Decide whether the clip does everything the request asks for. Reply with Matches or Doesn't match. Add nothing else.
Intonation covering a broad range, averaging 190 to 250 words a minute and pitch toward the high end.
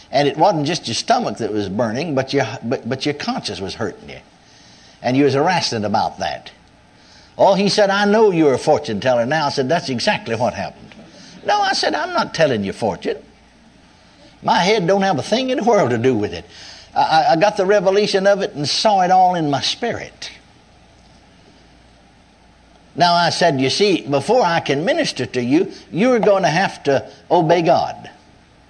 Doesn't match